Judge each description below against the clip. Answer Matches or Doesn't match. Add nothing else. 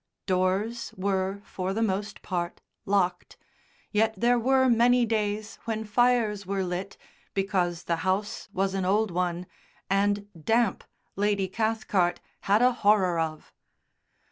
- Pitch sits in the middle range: Doesn't match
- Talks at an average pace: Doesn't match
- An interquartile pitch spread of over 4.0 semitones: Doesn't match